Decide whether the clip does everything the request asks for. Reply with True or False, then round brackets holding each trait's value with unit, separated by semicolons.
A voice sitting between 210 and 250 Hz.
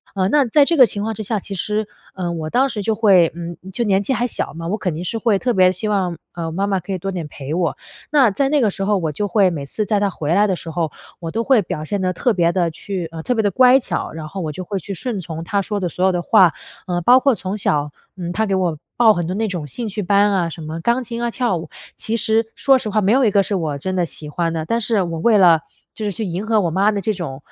False (195 Hz)